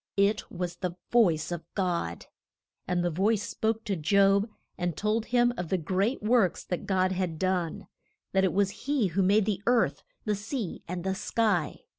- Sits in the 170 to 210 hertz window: Yes, high, 190 Hz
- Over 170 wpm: Yes, average, 180 wpm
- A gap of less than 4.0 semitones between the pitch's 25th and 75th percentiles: Yes, average, 3.4 semitones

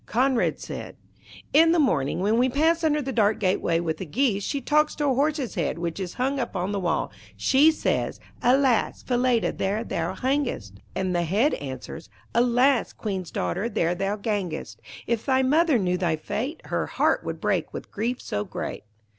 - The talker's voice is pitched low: No, high, 230 Hz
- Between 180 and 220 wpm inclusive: Yes, average, 185 wpm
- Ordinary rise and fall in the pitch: No, wide, 6.9 semitones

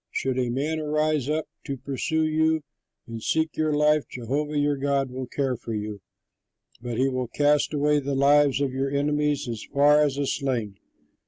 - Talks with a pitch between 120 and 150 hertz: Yes, medium, 140 Hz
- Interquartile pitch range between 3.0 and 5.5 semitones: No, narrow, 2.5 semitones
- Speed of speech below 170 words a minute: No, average, 175 wpm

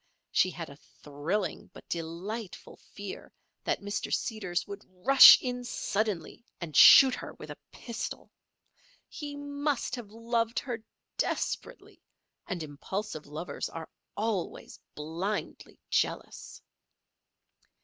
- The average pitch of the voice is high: Yes, high, 205 Hz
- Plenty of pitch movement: Yes, wide, 5.8 semitones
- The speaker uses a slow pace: Yes, slow, 110 wpm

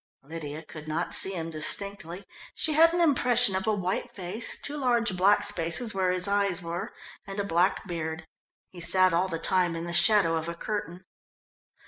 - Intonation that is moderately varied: Yes, average, 3.6 semitones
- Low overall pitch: No, medium, 185 Hz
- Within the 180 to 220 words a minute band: Yes, average, 185 wpm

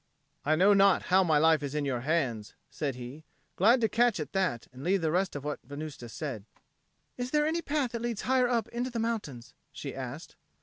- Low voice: No, medium, 175 Hz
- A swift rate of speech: Yes, fast, 215 wpm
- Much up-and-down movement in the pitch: Yes, wide, 8.5 semitones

